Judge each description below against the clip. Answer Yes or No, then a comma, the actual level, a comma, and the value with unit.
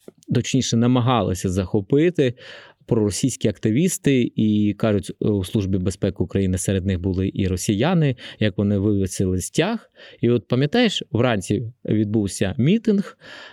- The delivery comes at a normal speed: Yes, average, 115 wpm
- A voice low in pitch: Yes, low, 110 Hz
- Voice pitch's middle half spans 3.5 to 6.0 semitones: Yes, average, 4.6 semitones